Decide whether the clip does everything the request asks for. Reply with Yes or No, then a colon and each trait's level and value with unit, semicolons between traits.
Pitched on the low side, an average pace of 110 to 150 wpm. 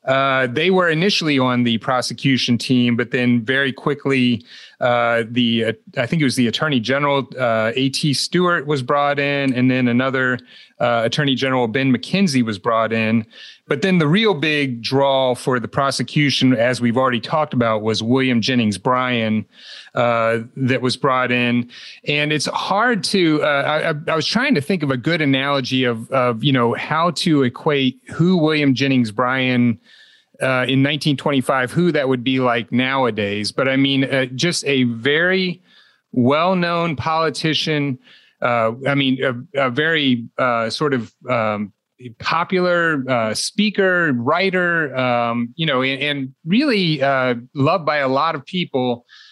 No: low, 130 Hz; average, 160 wpm